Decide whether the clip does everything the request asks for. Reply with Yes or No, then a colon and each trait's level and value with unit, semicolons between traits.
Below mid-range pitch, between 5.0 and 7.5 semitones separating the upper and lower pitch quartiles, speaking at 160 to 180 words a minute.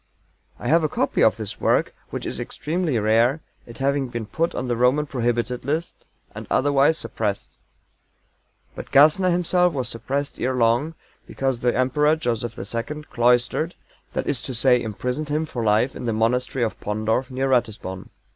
No: low, 125 Hz; average, 4.0 semitones; average, 165 wpm